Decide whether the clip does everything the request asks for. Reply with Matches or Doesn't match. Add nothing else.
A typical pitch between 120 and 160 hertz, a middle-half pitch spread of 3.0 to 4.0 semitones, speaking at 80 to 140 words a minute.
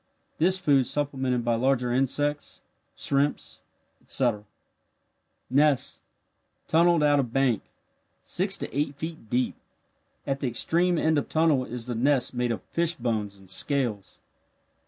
Matches